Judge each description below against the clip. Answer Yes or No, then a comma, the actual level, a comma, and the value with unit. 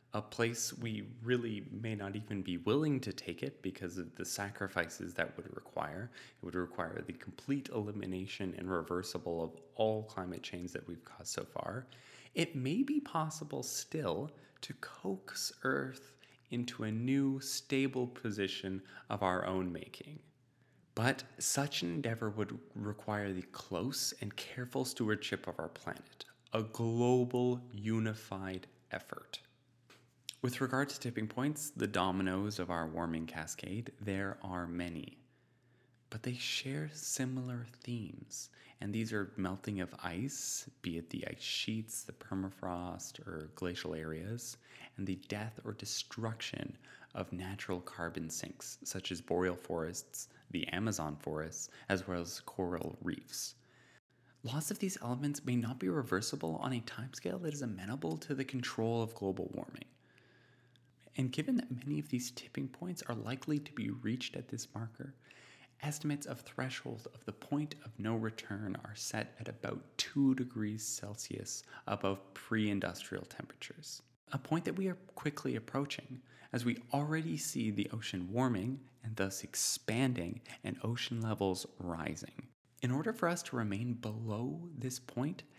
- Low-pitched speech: Yes, low, 115 Hz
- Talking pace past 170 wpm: No, average, 150 wpm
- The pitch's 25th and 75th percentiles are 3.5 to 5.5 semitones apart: Yes, average, 5.2 semitones